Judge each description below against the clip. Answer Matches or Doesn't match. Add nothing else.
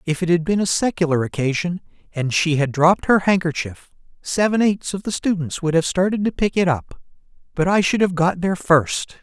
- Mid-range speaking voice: Matches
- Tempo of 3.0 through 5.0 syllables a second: Doesn't match